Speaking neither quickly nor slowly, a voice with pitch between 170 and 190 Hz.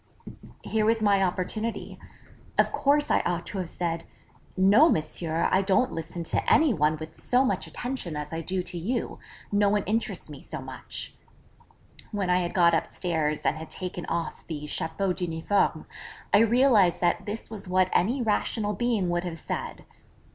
Yes: average, 170 wpm; medium, 185 Hz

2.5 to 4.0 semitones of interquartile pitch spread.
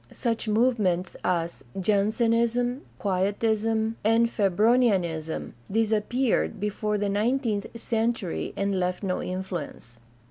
Yes: average, 3.4 semitones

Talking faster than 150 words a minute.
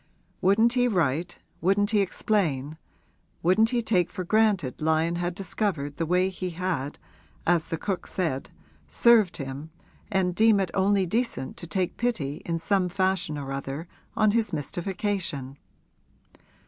No: average, 145 wpm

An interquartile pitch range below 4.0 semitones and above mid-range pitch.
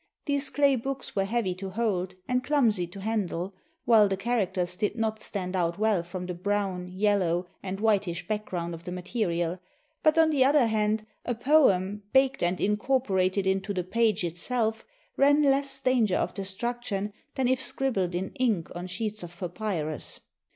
No: average, 4.9 semitones; high, 205 Hz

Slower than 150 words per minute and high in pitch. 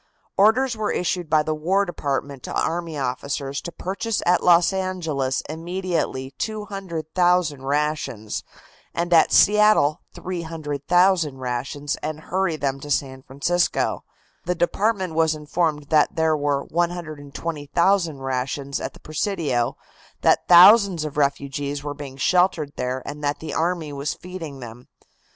No: slow, 135 wpm; medium, 155 Hz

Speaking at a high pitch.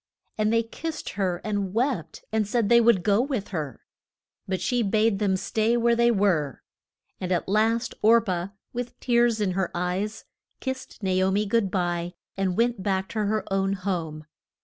Yes: high, 205 Hz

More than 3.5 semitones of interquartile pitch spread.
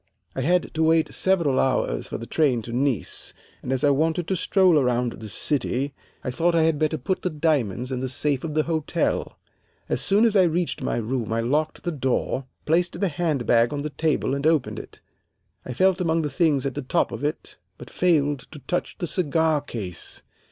Yes: average, 4.1 semitones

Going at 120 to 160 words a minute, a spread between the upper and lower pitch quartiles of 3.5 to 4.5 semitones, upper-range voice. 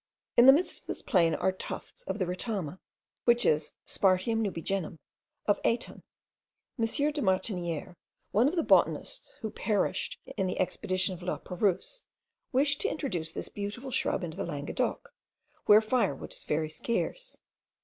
No: average, 150 wpm; average, 5.2 semitones; high, 200 Hz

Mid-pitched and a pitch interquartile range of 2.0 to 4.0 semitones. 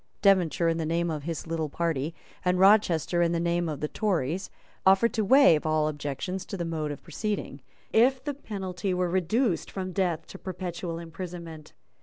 Yes: medium, 175 Hz; average, 2.9 semitones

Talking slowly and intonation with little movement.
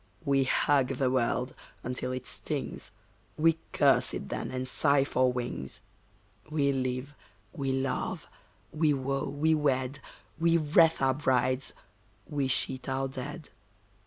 Yes: slow, 130 wpm; narrow, 2.1 semitones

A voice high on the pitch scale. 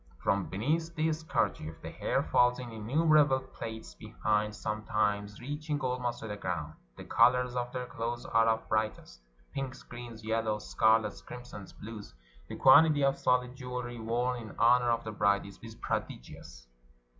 No: low, 115 Hz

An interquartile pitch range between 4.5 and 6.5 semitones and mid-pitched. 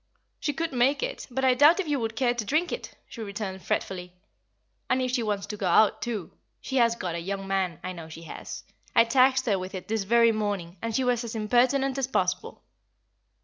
No: average, 5.0 semitones; high, 230 Hz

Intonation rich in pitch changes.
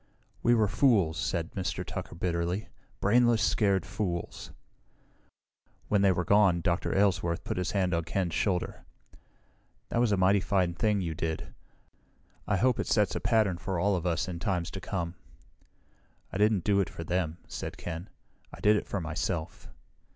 No: average, 3.2 semitones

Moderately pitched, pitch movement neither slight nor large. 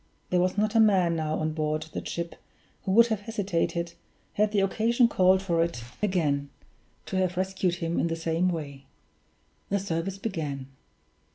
Yes: medium, 180 Hz; average, 3.3 semitones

